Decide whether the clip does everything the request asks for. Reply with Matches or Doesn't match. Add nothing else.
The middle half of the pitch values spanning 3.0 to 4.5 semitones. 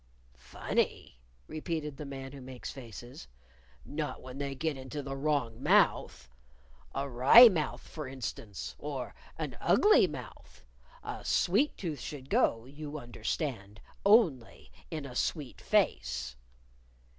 Matches